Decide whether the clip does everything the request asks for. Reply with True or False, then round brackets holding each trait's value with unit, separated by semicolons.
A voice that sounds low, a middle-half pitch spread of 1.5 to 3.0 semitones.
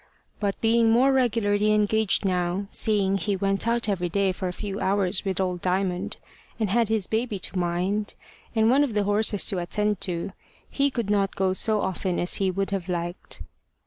False (200 Hz; 2.7 semitones)